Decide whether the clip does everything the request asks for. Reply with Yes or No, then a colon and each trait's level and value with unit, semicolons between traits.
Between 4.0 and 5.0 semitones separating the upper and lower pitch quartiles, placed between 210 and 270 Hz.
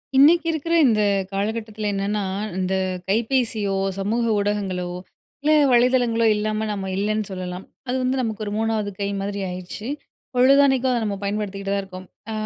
No: average, 3.3 semitones; high, 215 Hz